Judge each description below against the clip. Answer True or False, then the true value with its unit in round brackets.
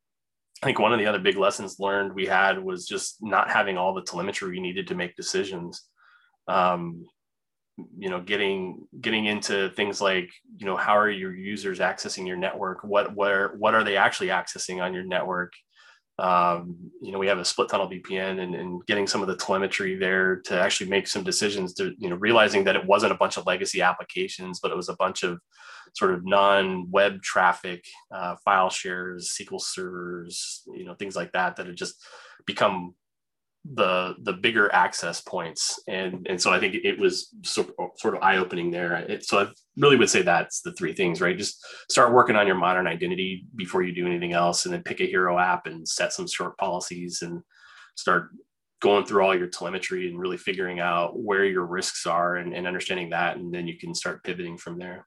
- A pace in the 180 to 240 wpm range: True (205 wpm)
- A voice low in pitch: True (95 Hz)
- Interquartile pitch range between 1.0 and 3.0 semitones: False (3.7 semitones)